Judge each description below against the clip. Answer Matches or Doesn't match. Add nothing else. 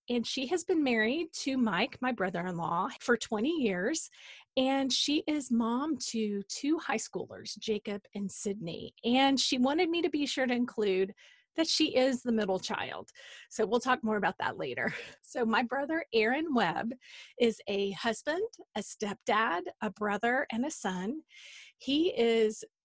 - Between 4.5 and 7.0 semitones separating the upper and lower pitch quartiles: Matches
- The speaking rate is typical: Matches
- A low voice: Doesn't match